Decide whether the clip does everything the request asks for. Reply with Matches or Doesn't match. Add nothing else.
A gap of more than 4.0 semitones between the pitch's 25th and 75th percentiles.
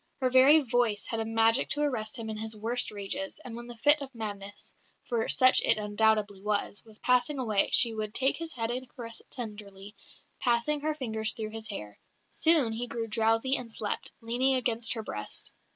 Doesn't match